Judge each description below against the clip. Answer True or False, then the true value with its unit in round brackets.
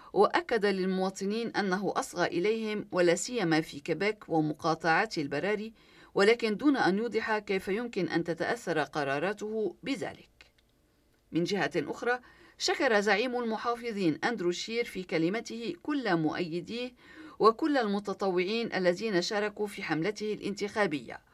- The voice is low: False (205 Hz)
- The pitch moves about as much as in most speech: True (4.6 semitones)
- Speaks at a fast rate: False (110 wpm)